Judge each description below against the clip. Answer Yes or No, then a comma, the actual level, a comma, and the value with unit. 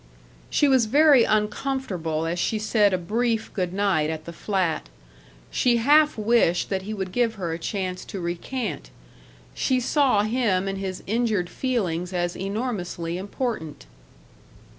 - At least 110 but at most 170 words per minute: Yes, average, 145 wpm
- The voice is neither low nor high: No, high, 200 Hz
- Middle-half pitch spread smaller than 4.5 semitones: No, average, 5.1 semitones